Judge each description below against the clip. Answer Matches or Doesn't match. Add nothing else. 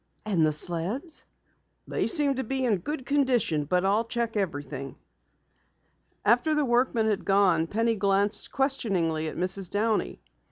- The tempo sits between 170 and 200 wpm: Doesn't match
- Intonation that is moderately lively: Doesn't match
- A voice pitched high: Matches